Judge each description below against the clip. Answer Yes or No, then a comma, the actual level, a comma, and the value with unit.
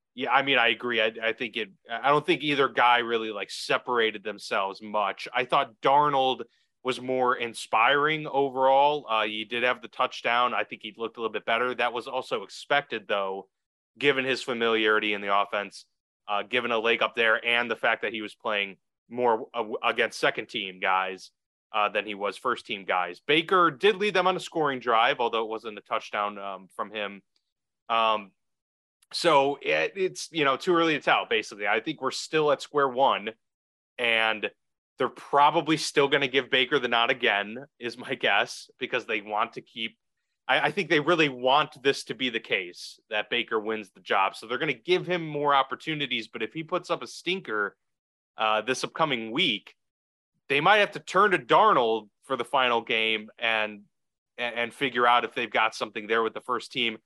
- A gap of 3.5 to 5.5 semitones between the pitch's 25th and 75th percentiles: Yes, average, 4.6 semitones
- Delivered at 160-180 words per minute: No, average, 200 wpm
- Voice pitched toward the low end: Yes, low, 120 Hz